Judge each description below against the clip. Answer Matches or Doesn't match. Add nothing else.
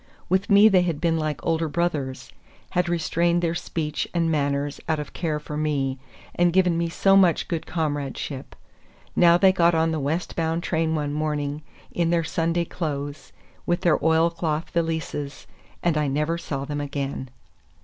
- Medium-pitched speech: Matches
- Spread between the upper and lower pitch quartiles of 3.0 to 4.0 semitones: Doesn't match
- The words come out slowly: Doesn't match